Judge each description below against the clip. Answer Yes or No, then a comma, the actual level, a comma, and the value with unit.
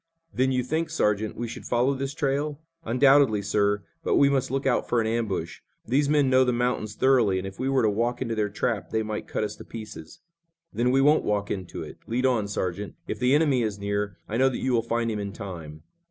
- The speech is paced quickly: Yes, fast, 235 wpm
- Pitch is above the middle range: No, low, 115 Hz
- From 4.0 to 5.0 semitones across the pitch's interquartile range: Yes, average, 4.3 semitones